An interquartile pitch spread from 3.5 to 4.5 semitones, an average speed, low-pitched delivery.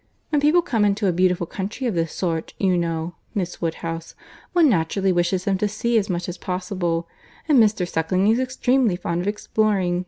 No: average, 3.8 semitones; average, 190 wpm; high, 190 Hz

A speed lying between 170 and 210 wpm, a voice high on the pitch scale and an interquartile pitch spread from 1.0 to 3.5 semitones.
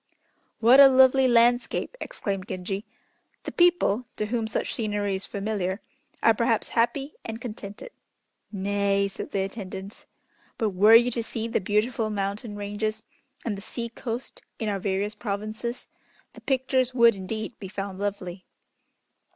No: average, 145 wpm; high, 215 Hz; average, 2.9 semitones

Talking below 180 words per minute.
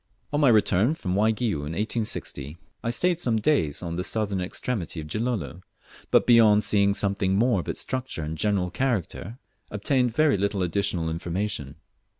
Yes: average, 160 wpm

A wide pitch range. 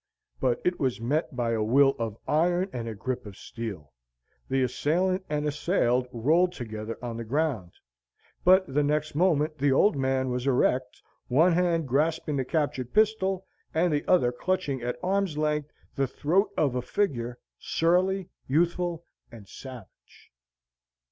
Yes: wide, 5.8 semitones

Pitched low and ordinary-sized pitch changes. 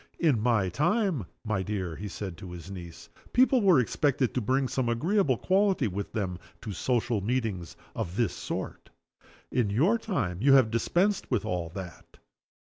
No: low, 115 Hz; wide, 7.0 semitones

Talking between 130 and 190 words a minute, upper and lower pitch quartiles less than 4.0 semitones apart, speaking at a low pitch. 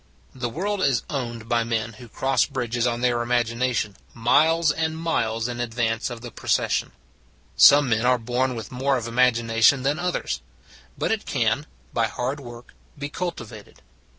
Yes: average, 165 wpm; average, 2.9 semitones; low, 120 Hz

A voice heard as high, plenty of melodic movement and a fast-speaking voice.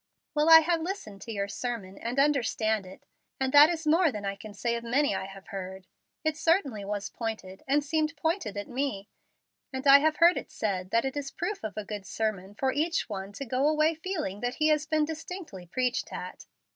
Yes: very high, 255 Hz; wide, 7.2 semitones; fast, 215 wpm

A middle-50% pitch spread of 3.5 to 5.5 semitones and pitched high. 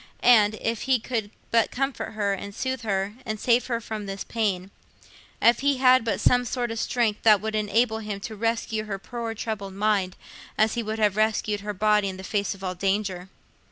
No: narrow, 2.5 semitones; high, 215 Hz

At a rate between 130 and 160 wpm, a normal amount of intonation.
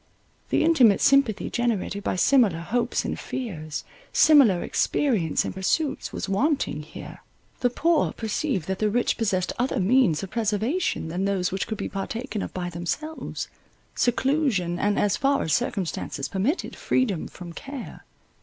No: average, 150 wpm; wide, 6.3 semitones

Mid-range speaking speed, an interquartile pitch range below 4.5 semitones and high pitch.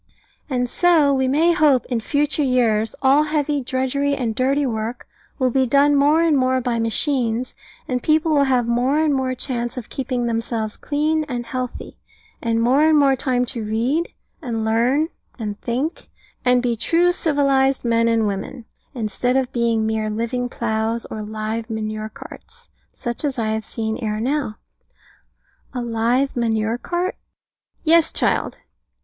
Yes: average, 160 wpm; average, 3.7 semitones; very high, 250 Hz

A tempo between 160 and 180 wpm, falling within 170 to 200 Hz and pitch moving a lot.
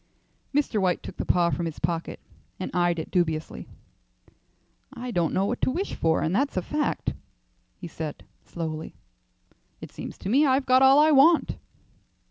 Yes: average, 170 wpm; high, 190 Hz; wide, 8.1 semitones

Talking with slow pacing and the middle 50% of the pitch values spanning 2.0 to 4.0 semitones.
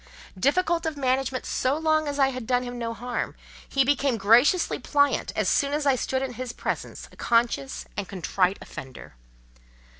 No: average, 175 wpm; average, 3.6 semitones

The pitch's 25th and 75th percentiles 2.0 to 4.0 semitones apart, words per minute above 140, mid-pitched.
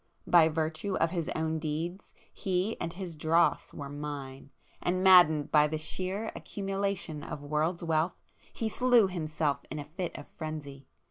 Yes: average, 3.4 semitones; average, 155 wpm; medium, 160 Hz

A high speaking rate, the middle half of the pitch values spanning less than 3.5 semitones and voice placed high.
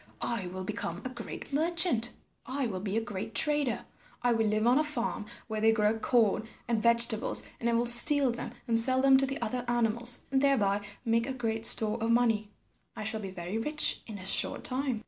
Yes: fast, 210 wpm; average, 3.0 semitones; high, 230 Hz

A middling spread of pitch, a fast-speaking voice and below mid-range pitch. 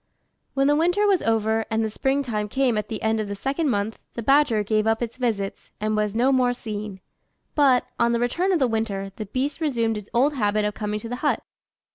No: average, 4.1 semitones; fast, 230 wpm; high, 225 Hz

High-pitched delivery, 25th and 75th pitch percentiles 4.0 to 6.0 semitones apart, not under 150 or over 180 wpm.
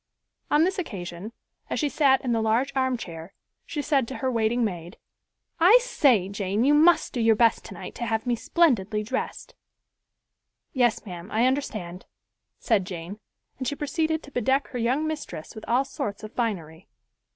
Yes: high, 235 Hz; wide, 5.4 semitones; average, 170 wpm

